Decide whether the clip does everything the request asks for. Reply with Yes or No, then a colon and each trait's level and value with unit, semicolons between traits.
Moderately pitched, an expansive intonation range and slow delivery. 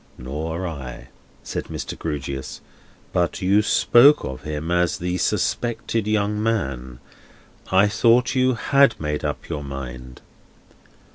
No: very low, 85 Hz; wide, 7.9 semitones; slow, 130 wpm